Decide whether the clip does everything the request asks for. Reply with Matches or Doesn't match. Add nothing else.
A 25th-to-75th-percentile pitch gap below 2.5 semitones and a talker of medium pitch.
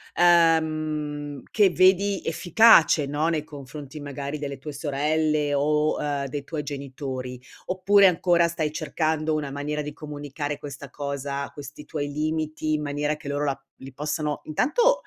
Matches